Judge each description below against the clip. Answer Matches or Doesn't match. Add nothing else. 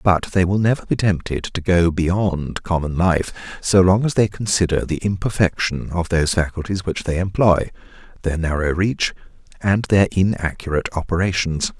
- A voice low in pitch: Matches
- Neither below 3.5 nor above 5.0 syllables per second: Matches